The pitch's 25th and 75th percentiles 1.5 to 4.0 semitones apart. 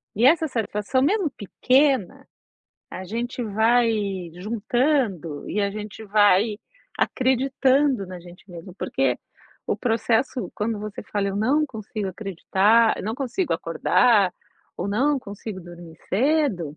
No: average, 4.6 semitones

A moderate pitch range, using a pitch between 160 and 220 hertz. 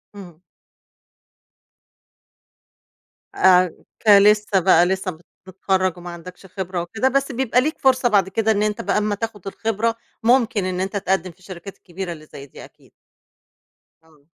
Yes: average, 3.4 semitones; high, 190 Hz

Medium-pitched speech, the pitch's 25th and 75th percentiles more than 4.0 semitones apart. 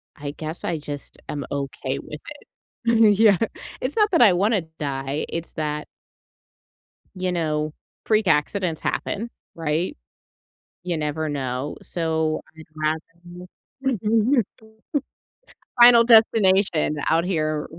Yes: medium, 165 Hz; wide, 5.6 semitones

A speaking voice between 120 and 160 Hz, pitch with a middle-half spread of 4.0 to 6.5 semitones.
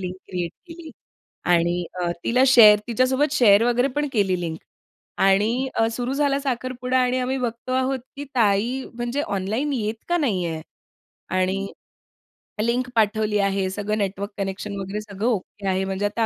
No: high, 220 Hz; average, 4.7 semitones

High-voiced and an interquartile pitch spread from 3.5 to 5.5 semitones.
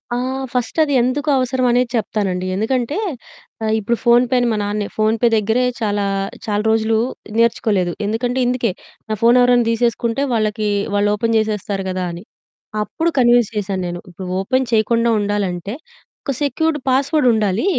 No: high, 225 Hz; average, 3.1 semitones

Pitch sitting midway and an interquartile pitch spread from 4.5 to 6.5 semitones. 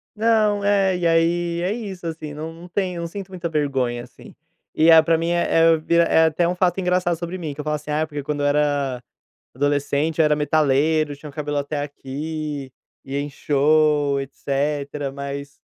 No: medium, 155 Hz; average, 2.9 semitones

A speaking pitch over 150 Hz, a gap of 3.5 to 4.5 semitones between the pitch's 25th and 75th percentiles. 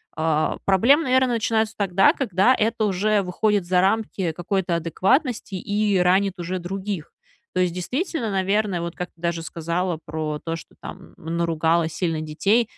Yes: medium, 185 Hz; average, 3.9 semitones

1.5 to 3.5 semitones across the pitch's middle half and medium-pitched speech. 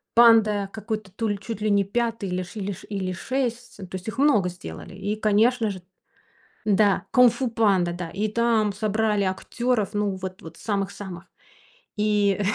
No: average, 2.8 semitones; high, 210 Hz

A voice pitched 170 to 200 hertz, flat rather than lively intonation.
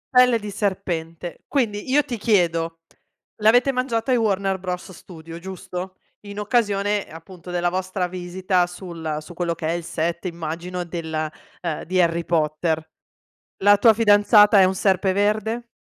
No: medium, 185 Hz; average, 3.4 semitones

